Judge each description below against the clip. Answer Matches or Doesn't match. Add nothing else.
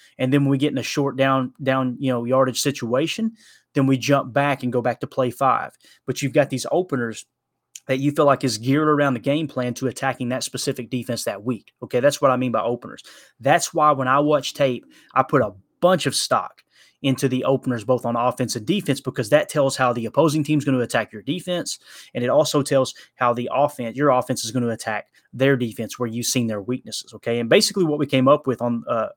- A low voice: Matches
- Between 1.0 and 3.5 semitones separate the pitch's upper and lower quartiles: Matches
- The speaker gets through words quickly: Matches